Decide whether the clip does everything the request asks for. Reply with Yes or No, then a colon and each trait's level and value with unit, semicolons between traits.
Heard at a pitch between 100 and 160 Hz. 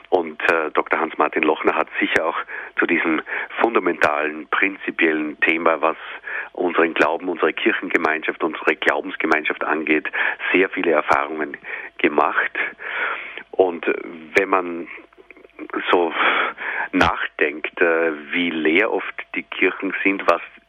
No: very low, 80 Hz